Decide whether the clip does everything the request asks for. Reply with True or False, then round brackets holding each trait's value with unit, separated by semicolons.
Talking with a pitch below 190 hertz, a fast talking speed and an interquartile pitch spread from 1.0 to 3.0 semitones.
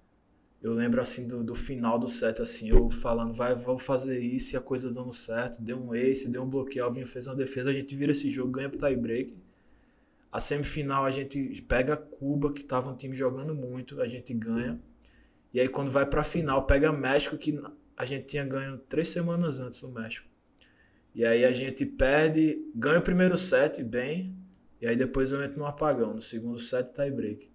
True (135 Hz; 200 wpm; 2.7 semitones)